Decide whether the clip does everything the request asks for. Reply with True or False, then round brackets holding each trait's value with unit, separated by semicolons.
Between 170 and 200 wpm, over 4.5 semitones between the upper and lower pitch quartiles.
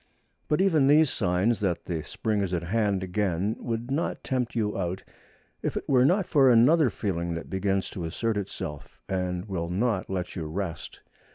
True (180 wpm; 5.1 semitones)